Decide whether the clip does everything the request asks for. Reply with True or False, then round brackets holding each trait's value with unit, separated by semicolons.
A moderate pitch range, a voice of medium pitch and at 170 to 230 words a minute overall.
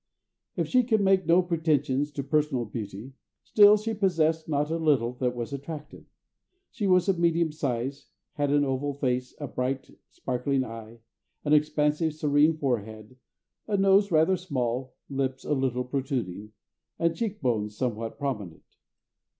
False (4.6 semitones; 145 Hz; 150 wpm)